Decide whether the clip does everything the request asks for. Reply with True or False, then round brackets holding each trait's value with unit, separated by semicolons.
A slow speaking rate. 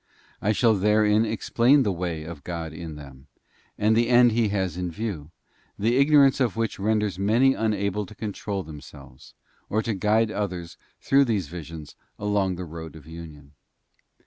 False (165 wpm)